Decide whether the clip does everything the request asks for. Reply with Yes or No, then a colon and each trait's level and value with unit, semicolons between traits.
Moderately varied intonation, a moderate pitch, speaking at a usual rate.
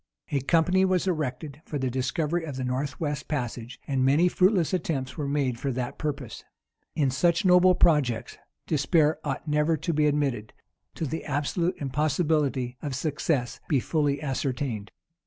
Yes: average, 3.5 semitones; medium, 145 Hz; average, 155 wpm